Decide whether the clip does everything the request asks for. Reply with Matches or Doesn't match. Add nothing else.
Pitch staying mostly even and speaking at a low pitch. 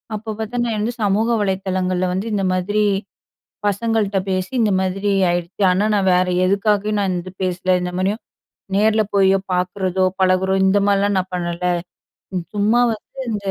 Doesn't match